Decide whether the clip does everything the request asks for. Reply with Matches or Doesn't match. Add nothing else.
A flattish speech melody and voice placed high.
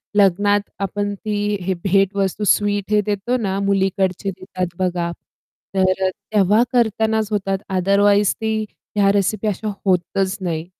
Matches